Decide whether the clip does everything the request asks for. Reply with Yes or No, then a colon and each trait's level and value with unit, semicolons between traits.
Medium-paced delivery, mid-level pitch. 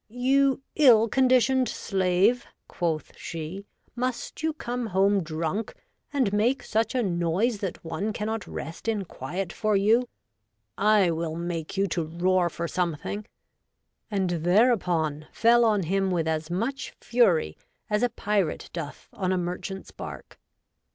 No: average, 150 wpm; high, 195 Hz